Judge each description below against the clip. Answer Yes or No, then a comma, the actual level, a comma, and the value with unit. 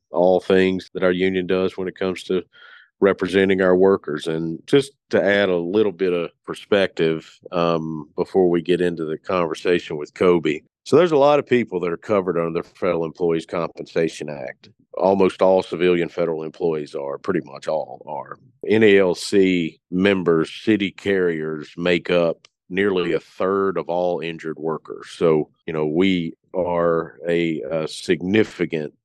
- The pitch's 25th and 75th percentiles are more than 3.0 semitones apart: No, narrow, 2.4 semitones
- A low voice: Yes, very low, 90 Hz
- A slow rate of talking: No, average, 160 wpm